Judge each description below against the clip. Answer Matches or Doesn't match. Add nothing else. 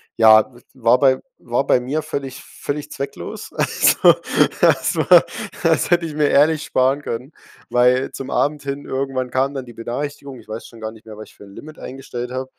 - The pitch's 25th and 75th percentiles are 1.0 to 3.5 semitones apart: Matches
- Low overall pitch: Matches